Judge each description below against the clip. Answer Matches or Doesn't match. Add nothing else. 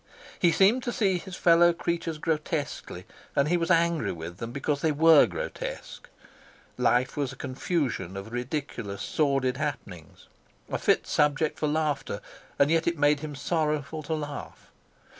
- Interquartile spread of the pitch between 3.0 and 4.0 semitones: Matches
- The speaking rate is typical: Matches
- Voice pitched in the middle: Matches